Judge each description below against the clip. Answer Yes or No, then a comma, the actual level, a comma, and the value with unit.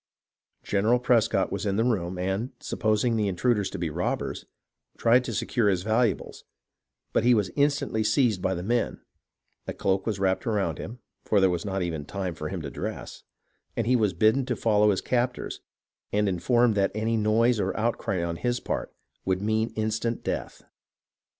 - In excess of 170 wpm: Yes, average, 180 wpm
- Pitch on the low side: Yes, low, 110 Hz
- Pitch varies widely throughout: No, average, 3.6 semitones